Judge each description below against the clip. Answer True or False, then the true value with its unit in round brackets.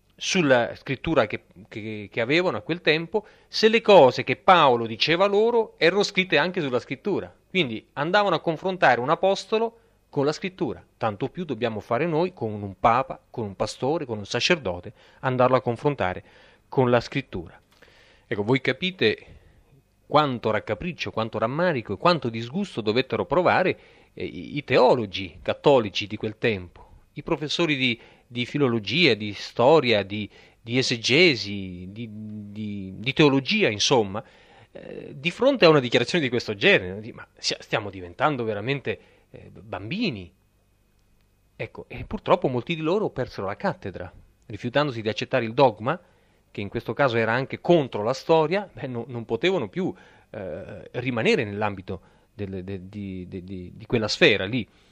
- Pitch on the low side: True (120 Hz)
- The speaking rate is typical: True (150 wpm)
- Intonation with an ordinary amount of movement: False (7.1 semitones)